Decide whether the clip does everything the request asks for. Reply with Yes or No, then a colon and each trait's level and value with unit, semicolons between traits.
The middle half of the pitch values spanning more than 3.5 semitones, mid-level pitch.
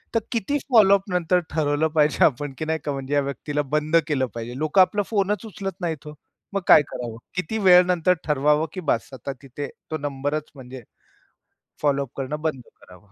Yes: average, 4.7 semitones; medium, 150 Hz